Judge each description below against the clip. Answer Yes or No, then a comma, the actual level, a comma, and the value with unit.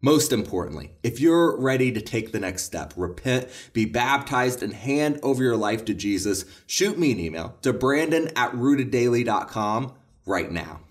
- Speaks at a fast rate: No, average, 165 wpm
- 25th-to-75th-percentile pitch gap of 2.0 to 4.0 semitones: No, average, 4.8 semitones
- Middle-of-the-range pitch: No, low, 120 Hz